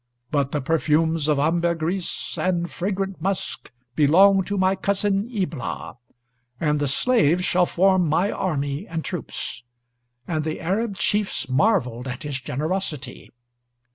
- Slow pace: Yes, slow, 130 wpm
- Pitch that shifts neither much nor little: Yes, average, 4.5 semitones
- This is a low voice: No, medium, 170 Hz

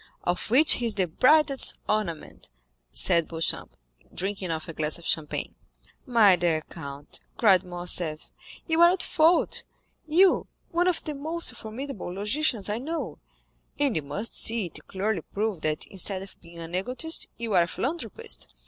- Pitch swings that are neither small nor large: No, wide, 8.3 semitones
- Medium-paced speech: Yes, average, 155 wpm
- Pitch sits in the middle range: No, high, 205 Hz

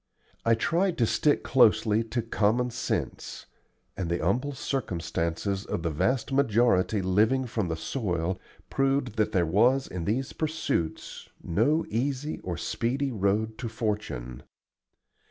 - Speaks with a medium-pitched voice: No, low, 110 Hz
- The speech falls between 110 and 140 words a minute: Yes, slow, 135 wpm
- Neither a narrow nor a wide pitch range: No, wide, 6.0 semitones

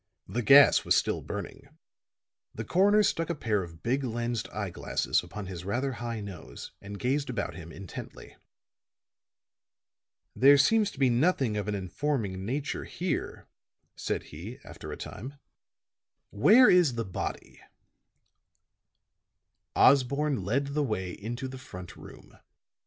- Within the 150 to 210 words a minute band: No, slow, 135 wpm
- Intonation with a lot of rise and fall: Yes, wide, 5.7 semitones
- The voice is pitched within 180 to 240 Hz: No, low, 120 Hz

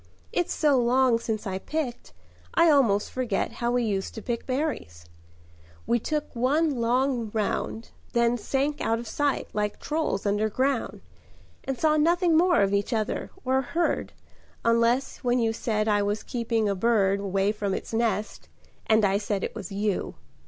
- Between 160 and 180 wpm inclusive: Yes, average, 165 wpm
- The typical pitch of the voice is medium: No, high, 230 Hz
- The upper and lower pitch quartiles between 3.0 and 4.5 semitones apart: Yes, average, 4.2 semitones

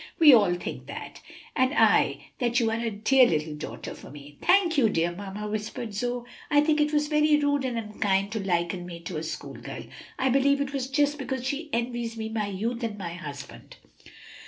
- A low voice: No, high, 230 Hz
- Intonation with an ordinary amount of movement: No, wide, 5.9 semitones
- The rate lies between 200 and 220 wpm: Yes, fast, 205 wpm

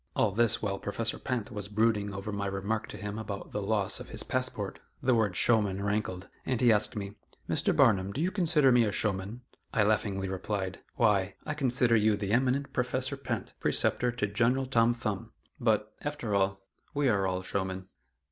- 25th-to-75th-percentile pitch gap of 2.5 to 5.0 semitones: Yes, average, 3.5 semitones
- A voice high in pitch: No, low, 105 Hz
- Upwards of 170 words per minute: Yes, average, 185 wpm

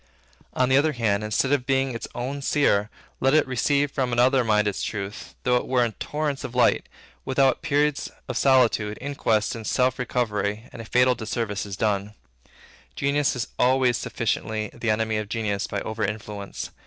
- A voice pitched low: Yes, low, 120 Hz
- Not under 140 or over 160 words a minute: No, average, 180 wpm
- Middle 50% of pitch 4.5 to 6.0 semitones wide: No, average, 3.8 semitones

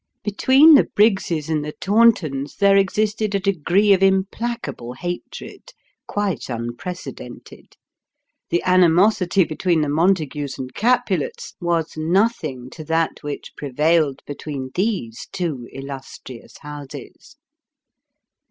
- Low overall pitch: No, medium, 170 Hz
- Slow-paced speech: Yes, slow, 105 wpm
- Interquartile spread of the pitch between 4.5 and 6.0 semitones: Yes, wide, 5.6 semitones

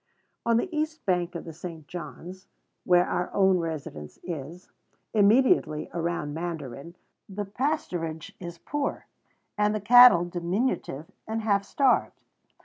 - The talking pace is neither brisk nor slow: No, slow, 130 wpm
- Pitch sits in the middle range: Yes, medium, 180 Hz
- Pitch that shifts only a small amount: No, average, 4.5 semitones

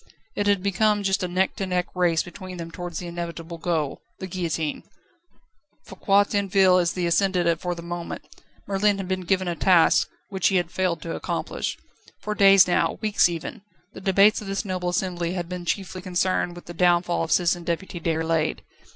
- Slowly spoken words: No, average, 190 wpm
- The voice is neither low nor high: Yes, medium, 180 Hz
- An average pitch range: No, narrow, 2.0 semitones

